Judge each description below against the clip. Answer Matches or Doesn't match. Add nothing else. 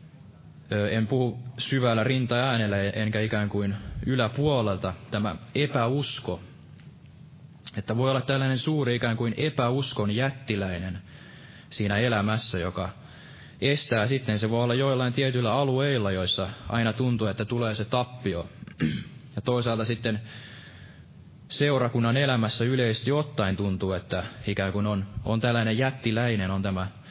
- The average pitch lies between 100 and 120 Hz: Matches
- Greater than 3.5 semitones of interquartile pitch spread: Matches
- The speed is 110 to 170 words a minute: Matches